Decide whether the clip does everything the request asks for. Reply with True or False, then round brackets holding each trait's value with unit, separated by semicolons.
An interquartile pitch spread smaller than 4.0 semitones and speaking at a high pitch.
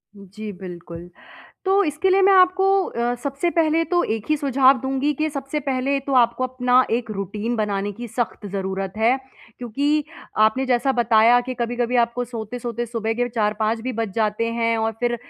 True (3.6 semitones; 240 Hz)